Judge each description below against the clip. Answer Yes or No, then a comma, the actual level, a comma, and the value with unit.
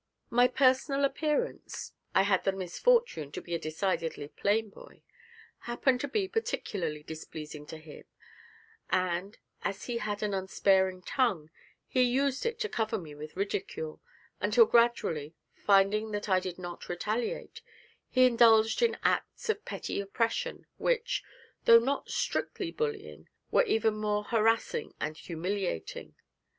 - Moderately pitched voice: No, high, 210 Hz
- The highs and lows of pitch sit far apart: Yes, wide, 6.1 semitones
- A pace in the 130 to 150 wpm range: Yes, average, 140 wpm